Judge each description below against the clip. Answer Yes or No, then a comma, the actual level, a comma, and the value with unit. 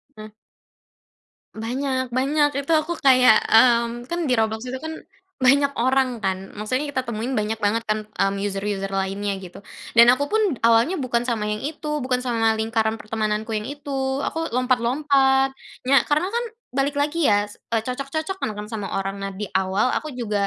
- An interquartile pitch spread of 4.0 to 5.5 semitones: Yes, average, 4.3 semitones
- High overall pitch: Yes, high, 240 Hz